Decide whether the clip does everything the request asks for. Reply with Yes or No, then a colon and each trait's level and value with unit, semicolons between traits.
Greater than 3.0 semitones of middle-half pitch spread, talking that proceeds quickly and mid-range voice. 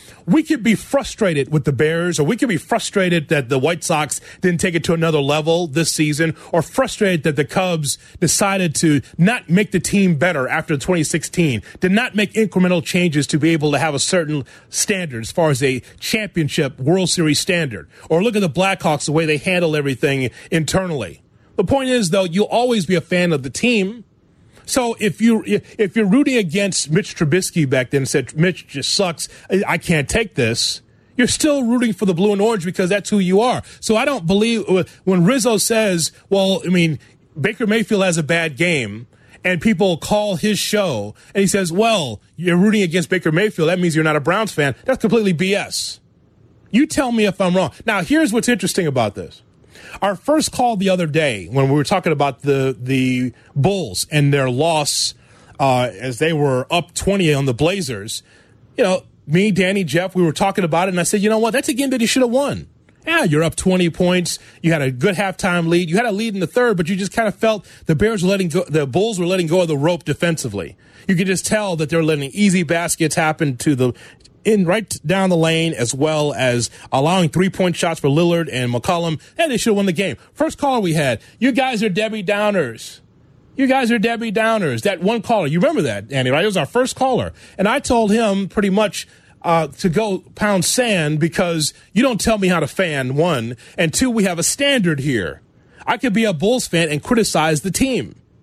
Yes: wide, 5.4 semitones; fast, 215 wpm; medium, 180 Hz